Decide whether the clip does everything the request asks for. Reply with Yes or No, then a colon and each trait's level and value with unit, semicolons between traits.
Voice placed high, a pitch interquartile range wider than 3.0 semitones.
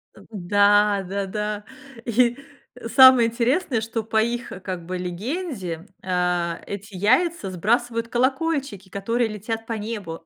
Yes: high, 215 Hz; average, 3.8 semitones